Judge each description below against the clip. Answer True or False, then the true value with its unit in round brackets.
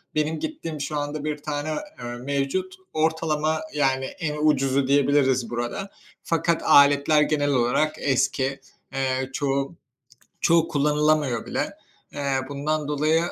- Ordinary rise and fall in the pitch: False (2.2 semitones)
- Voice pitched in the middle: True (145 Hz)